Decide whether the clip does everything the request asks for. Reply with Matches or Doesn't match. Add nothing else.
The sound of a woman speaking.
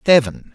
Doesn't match